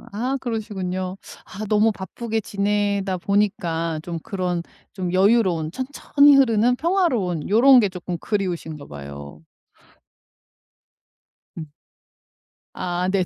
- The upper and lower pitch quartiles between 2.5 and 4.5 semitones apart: Yes, average, 4.2 semitones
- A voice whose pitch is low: No, high, 195 Hz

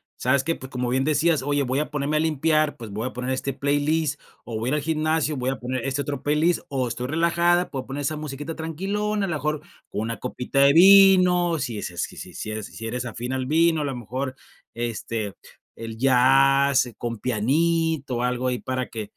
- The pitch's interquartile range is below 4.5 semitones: Yes, average, 3.9 semitones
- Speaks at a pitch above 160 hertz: No, medium, 140 Hz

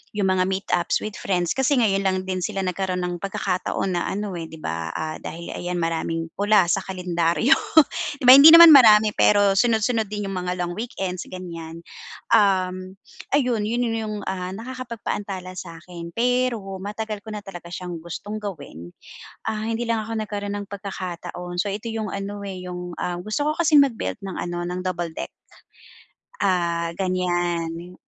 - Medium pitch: No, high, 195 Hz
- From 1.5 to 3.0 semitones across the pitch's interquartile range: No, average, 3.4 semitones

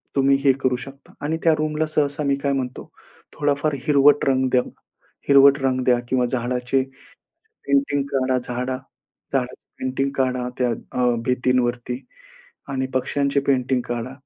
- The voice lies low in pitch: Yes, low, 130 Hz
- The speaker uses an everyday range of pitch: No, narrow, 1.8 semitones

